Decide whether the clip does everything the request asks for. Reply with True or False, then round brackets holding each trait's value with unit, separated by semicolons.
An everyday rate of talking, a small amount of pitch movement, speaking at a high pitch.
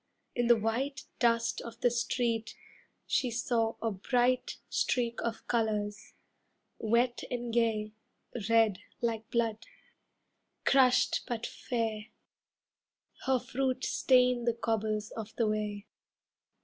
False (110 wpm; 1.7 semitones; 230 Hz)